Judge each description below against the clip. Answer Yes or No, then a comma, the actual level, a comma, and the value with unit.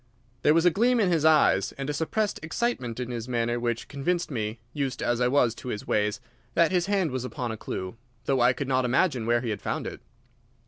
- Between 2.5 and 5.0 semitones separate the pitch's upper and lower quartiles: No, wide, 5.4 semitones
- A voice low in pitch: Yes, low, 130 Hz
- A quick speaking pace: Yes, fast, 230 wpm